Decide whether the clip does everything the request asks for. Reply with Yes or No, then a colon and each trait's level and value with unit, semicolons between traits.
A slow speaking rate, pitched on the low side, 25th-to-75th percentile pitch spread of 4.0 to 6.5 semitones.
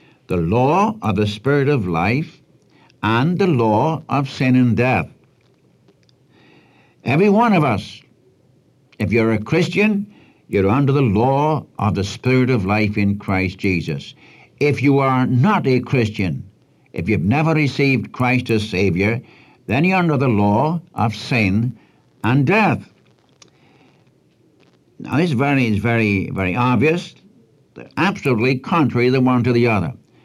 No: average, 145 wpm; low, 125 Hz; average, 5.1 semitones